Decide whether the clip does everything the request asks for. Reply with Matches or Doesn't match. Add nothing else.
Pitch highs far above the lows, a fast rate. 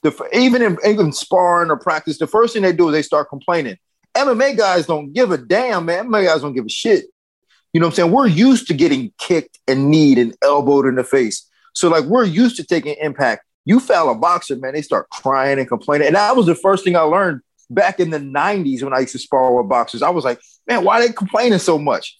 Matches